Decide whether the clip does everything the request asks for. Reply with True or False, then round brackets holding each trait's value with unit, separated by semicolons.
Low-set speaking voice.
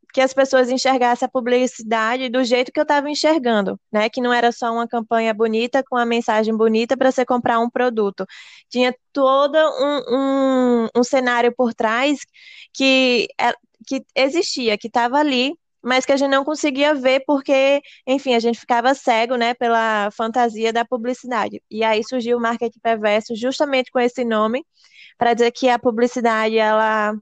False (250 Hz)